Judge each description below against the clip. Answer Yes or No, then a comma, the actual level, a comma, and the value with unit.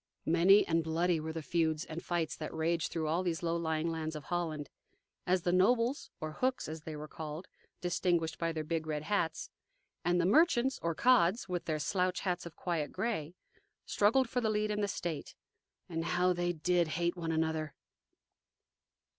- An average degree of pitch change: No, narrow, 2.3 semitones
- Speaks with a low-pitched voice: No, medium, 170 Hz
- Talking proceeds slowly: No, average, 185 wpm